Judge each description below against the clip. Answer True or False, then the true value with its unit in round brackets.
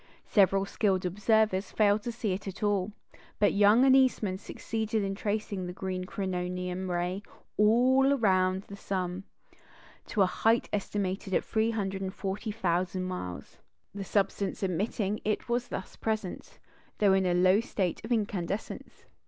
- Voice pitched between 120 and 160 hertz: False (195 Hz)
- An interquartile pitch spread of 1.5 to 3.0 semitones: True (2.6 semitones)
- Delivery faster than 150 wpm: False (140 wpm)